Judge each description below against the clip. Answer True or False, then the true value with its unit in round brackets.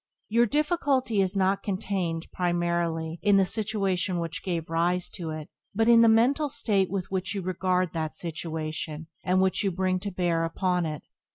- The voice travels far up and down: False (3.2 semitones)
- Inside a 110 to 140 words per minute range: False (175 wpm)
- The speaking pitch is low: False (185 Hz)